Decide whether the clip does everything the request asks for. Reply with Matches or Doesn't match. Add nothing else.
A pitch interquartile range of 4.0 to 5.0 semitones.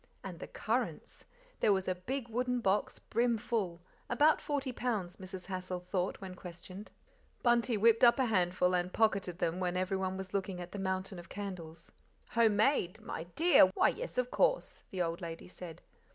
Matches